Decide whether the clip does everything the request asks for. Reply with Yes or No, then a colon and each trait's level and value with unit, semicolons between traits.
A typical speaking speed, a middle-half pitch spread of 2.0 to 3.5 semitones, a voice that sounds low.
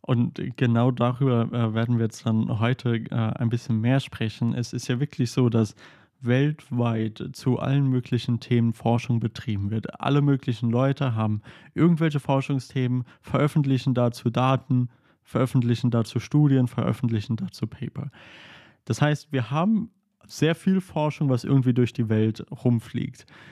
Yes: average, 140 wpm; average, 2.8 semitones; low, 125 Hz